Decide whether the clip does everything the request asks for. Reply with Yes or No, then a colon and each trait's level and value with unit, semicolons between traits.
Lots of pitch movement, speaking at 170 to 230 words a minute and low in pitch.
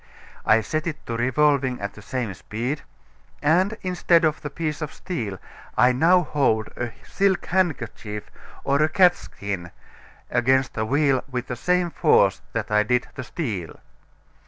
No: wide, 5.9 semitones; average, 155 wpm; low, 130 Hz